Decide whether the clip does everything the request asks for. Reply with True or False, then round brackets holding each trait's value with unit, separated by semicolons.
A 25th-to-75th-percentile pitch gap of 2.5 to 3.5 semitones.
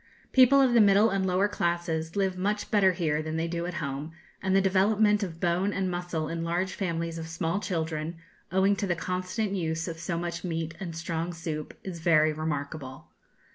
True (2.9 semitones)